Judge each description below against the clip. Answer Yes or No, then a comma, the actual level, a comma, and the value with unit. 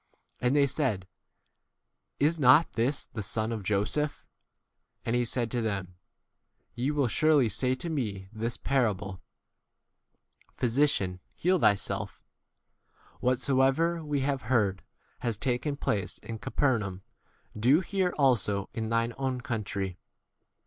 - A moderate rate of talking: No, slow, 130 wpm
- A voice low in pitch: Yes, low, 125 Hz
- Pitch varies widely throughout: No, average, 4.7 semitones